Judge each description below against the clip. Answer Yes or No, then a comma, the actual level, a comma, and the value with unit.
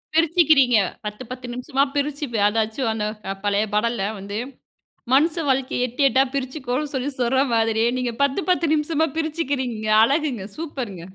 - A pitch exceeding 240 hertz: Yes, very high, 260 Hz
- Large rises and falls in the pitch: No, average, 4.5 semitones